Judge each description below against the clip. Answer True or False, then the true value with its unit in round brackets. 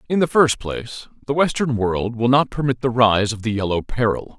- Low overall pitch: True (120 Hz)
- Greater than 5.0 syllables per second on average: True (5.2 syllables/s)